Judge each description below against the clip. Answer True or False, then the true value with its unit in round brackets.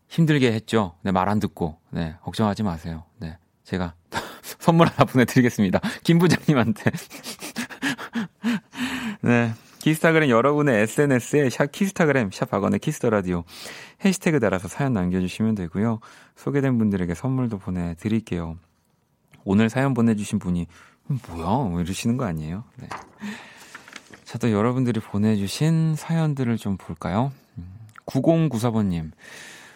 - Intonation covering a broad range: True (7.4 semitones)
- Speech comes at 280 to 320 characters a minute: True (295 characters per minute)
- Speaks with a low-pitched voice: True (115 Hz)